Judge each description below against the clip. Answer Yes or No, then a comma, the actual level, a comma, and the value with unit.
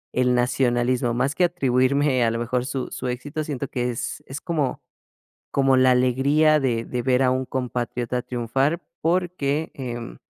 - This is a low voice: Yes, low, 130 Hz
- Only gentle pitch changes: Yes, narrow, 2.3 semitones